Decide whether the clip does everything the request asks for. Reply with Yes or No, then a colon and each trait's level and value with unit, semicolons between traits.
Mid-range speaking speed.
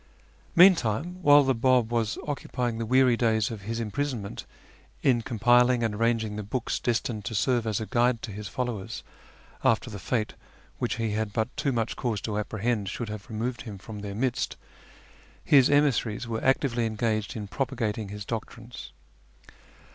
Yes: average, 170 wpm